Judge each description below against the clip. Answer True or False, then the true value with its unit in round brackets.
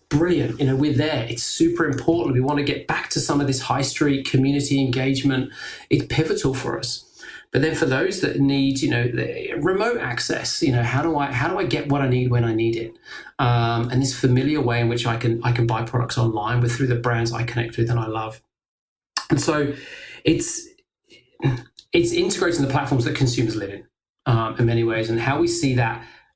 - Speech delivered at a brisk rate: True (220 wpm)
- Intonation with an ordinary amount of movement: True (3.6 semitones)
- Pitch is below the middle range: True (130 Hz)